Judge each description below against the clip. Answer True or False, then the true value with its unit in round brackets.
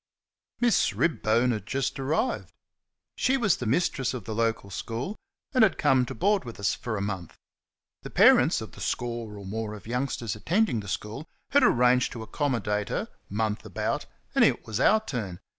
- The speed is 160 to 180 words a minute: True (175 wpm)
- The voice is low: True (120 Hz)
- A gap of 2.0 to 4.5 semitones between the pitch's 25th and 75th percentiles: False (5.1 semitones)